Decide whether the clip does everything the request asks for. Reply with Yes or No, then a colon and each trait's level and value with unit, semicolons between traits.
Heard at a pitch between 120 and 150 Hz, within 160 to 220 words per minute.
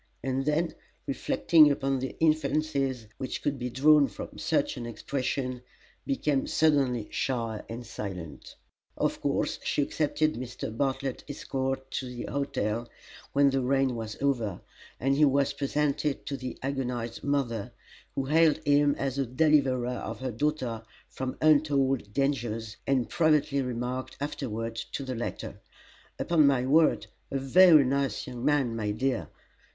No: low, 135 Hz; average, 145 wpm